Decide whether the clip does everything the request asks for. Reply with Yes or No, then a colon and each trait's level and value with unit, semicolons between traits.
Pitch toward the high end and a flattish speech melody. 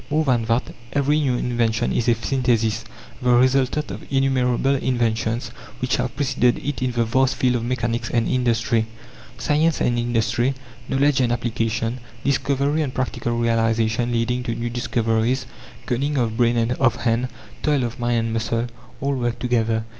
No: low, 120 Hz; narrow, 2.3 semitones